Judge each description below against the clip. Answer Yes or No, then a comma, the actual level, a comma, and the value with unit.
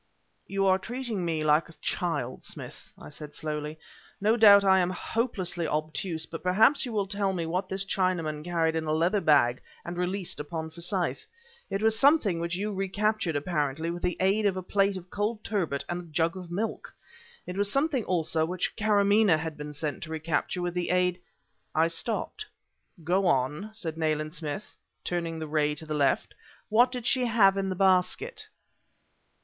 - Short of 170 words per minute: No, average, 185 wpm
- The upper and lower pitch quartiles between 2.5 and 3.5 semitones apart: No, average, 4.0 semitones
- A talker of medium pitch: Yes, medium, 180 Hz